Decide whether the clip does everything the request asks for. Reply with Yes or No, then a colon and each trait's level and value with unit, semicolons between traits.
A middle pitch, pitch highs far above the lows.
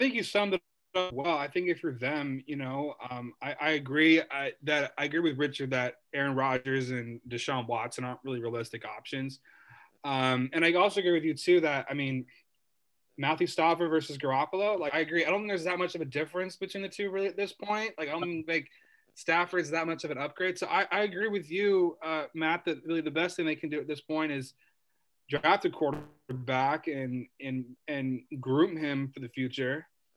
No: medium, 155 Hz; average, 4.7 semitones